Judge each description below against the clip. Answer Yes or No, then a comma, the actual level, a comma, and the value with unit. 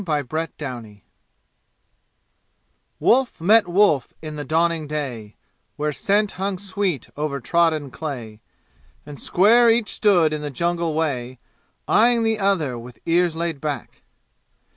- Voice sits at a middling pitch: Yes, medium, 160 Hz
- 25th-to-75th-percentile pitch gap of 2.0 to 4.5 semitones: No, wide, 5.4 semitones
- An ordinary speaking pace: No, slow, 125 wpm